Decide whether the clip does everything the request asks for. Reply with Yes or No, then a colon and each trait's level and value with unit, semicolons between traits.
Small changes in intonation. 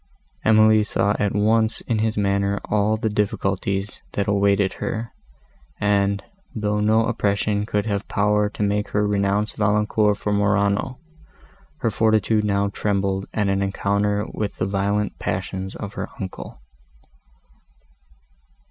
Yes: narrow, 1.1 semitones